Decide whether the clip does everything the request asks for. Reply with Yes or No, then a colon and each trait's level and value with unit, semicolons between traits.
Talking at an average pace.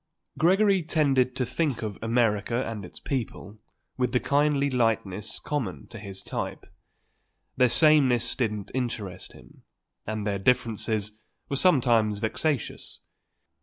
No: slow, 125 wpm